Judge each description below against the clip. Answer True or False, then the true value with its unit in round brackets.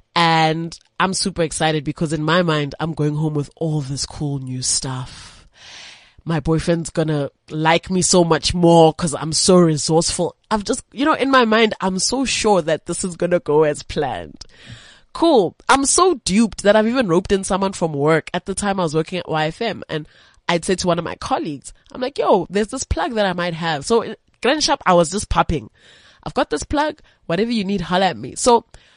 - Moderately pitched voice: True (175 Hz)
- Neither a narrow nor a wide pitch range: True (4.7 semitones)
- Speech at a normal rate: False (215 wpm)